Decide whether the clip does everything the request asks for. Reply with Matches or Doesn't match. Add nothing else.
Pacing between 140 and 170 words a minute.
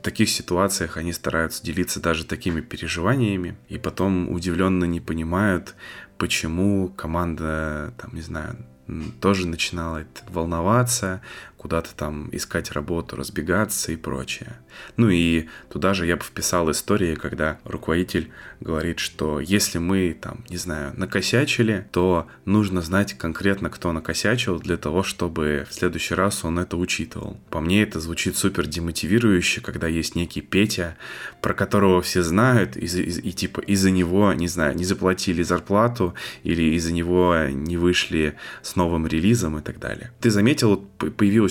Matches